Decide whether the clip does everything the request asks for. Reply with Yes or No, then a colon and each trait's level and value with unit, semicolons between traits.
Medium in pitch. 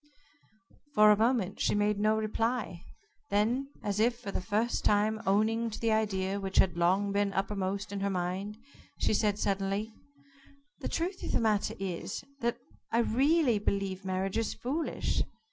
No: high, 210 Hz